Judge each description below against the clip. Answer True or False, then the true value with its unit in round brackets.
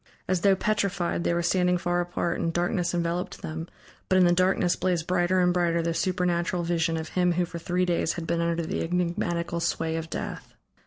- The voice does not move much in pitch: True (1.1 semitones)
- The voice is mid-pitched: True (175 Hz)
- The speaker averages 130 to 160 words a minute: False (205 wpm)